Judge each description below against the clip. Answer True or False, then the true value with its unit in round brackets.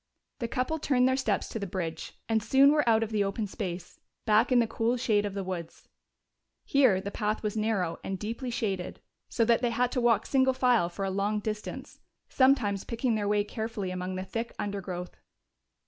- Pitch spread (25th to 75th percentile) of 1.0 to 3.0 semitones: False (3.6 semitones)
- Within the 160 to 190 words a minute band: False (200 wpm)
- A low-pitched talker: False (215 Hz)